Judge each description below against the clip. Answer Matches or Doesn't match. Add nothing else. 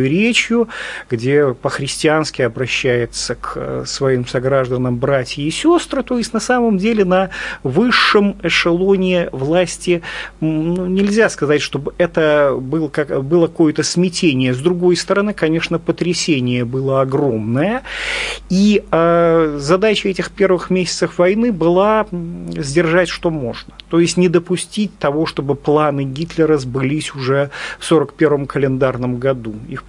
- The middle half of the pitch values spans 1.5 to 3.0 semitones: Doesn't match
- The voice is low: Doesn't match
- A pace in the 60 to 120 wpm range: Matches